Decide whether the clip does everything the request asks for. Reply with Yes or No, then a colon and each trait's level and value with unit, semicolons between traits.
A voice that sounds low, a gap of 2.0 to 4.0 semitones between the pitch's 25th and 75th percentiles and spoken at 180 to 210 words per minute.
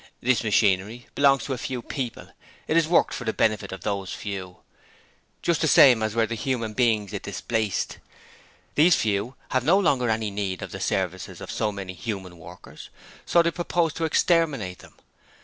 No: low, 115 Hz; wide, 5.6 semitones; average, 185 wpm